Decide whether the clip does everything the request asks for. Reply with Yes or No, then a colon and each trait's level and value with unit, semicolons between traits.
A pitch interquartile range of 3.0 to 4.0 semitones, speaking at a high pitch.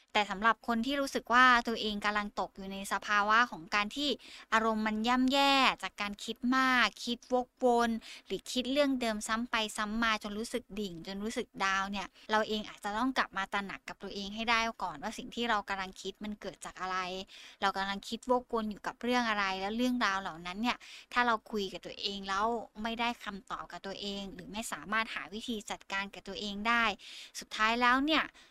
Yes: average, 3.3 semitones; high, 215 Hz